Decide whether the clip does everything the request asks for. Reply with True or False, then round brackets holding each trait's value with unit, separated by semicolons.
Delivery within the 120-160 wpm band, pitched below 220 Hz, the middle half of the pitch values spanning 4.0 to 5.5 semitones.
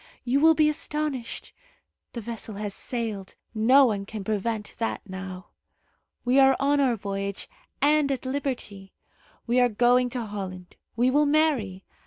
False (150 wpm; 235 Hz; 5.2 semitones)